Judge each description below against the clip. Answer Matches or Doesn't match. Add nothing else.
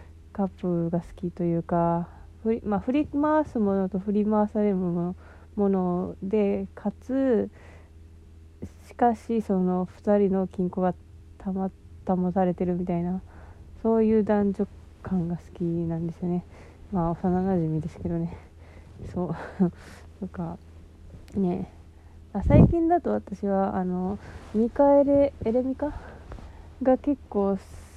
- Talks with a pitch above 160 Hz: Matches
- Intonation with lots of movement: Doesn't match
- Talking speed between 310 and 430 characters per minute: Doesn't match